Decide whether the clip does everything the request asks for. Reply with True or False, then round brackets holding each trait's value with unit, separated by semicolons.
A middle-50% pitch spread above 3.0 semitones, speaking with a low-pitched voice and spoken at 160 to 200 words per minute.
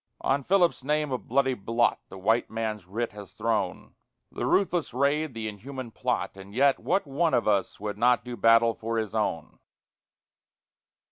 True (4.4 semitones; 115 Hz; 165 wpm)